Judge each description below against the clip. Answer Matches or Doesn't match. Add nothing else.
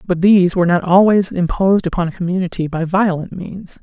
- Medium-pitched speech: Matches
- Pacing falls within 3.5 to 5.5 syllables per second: Doesn't match